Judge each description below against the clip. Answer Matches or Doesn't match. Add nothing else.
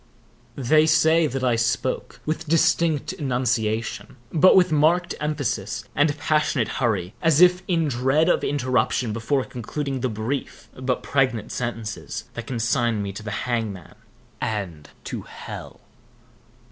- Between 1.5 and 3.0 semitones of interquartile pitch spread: Doesn't match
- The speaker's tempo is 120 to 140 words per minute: Matches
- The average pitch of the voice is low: Matches